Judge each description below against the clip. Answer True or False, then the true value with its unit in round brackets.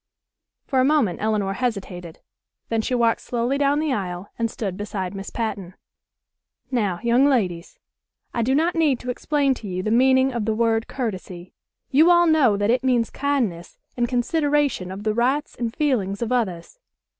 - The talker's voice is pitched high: True (235 Hz)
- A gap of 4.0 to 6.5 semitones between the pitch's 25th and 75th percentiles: True (5.0 semitones)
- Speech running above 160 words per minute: True (175 wpm)